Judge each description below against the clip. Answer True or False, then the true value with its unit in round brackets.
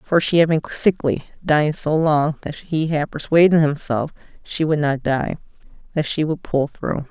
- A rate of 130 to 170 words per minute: False (185 wpm)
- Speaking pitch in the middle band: True (155 Hz)